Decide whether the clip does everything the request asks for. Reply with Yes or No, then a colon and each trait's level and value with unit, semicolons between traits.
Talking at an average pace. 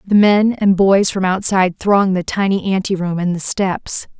Yes: average, 185 wpm